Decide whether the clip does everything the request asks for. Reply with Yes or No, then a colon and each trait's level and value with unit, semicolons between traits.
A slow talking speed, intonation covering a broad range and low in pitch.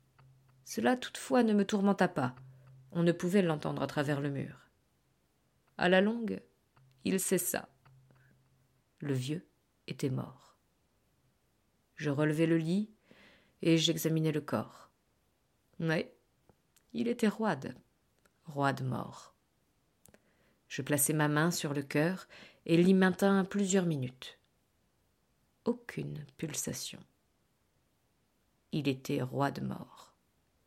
No: slow, 110 wpm; wide, 5.8 semitones; medium, 150 Hz